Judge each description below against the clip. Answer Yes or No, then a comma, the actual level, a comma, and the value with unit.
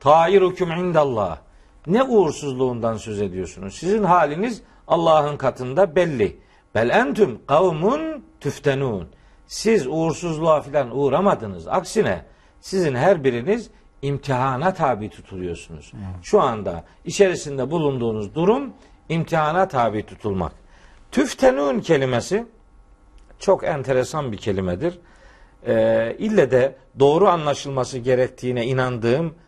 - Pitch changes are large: Yes, wide, 7.5 semitones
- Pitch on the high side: No, medium, 140 Hz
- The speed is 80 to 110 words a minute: Yes, slow, 95 wpm